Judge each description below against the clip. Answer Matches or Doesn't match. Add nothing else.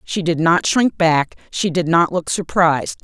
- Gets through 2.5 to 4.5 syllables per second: Matches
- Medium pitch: Matches